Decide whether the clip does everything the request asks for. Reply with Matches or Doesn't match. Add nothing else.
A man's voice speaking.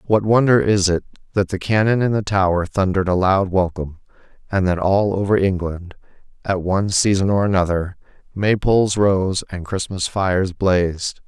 Matches